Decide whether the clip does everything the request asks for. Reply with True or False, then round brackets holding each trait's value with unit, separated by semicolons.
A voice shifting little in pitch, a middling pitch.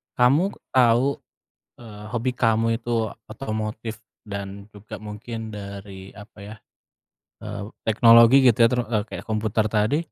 False (2.1 semitones; 110 Hz)